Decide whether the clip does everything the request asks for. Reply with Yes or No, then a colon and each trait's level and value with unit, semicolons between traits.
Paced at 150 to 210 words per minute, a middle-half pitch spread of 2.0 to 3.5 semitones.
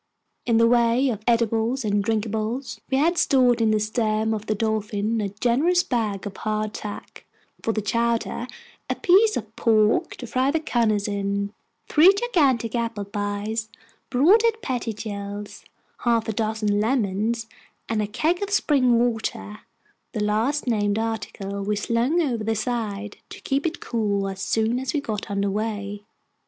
Yes: average, 160 wpm; average, 2.9 semitones